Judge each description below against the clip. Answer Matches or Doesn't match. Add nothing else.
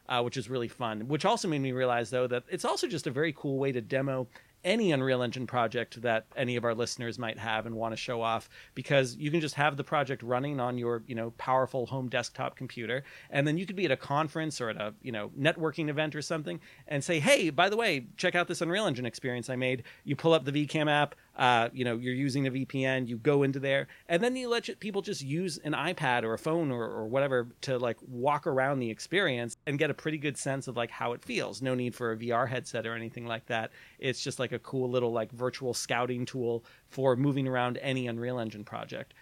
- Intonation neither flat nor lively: Matches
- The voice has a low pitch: Matches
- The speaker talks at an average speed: Doesn't match